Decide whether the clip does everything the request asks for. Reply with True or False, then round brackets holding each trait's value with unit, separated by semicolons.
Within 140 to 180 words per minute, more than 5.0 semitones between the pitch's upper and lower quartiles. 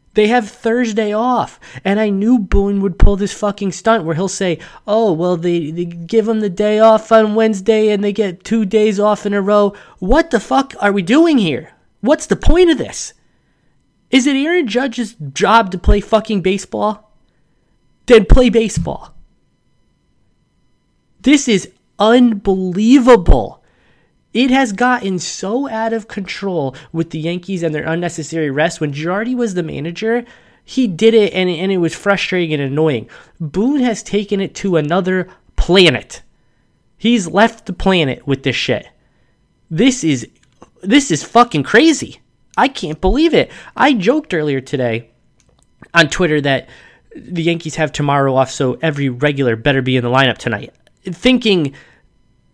True (160 wpm; 5.5 semitones)